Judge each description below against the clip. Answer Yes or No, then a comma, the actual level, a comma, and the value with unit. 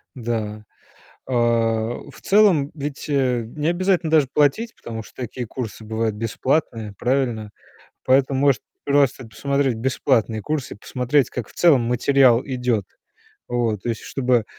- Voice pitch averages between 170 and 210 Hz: No, low, 130 Hz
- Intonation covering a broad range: No, average, 3.7 semitones